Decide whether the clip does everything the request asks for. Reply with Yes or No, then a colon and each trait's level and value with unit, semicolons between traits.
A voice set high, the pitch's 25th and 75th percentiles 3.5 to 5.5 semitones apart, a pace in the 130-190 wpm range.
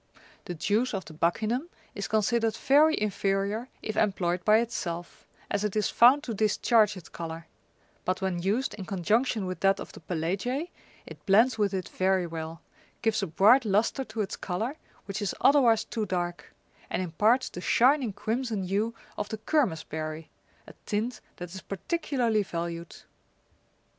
Yes: high, 205 Hz; average, 4.2 semitones; average, 165 wpm